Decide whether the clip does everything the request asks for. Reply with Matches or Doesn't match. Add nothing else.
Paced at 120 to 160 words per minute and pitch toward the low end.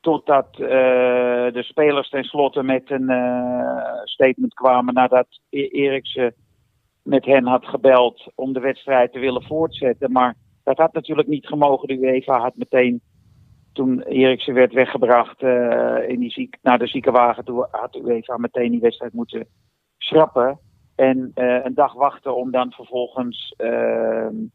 Matches